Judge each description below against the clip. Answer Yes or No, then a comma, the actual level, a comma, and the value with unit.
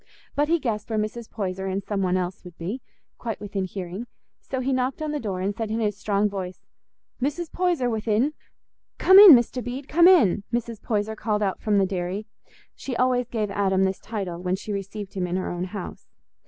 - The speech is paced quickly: Yes, fast, 210 wpm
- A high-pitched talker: Yes, high, 210 Hz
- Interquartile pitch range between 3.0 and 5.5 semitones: Yes, average, 4.4 semitones